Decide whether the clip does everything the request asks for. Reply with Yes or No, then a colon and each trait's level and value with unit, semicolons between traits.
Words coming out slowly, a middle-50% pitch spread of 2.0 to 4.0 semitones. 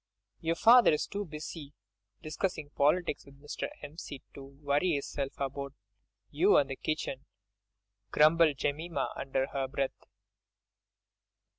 Yes: slow, 120 wpm; narrow, 2.6 semitones